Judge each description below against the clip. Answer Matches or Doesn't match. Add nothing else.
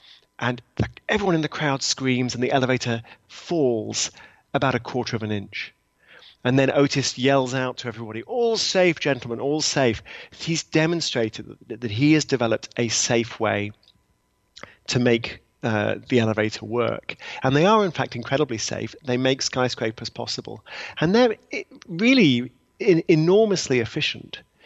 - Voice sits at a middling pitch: Doesn't match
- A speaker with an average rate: Matches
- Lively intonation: Doesn't match